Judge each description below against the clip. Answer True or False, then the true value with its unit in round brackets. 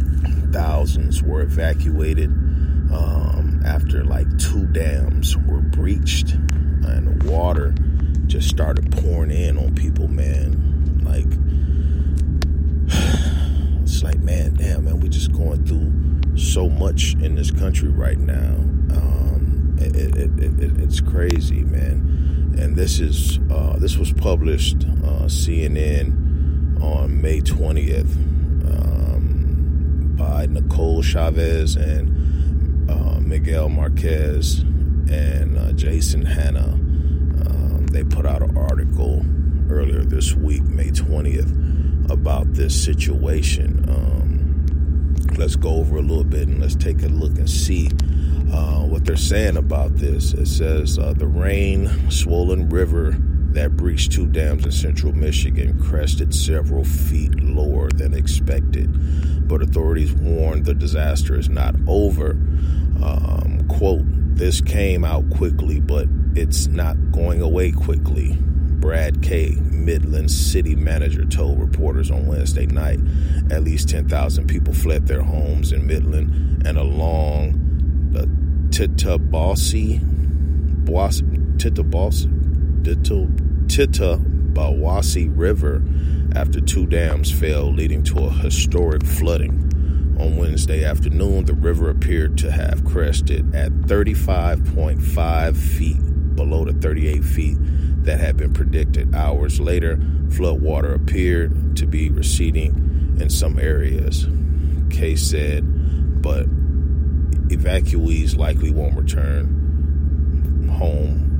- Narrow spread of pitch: True (0.5 semitones)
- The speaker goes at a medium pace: False (115 wpm)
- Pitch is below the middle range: True (75 Hz)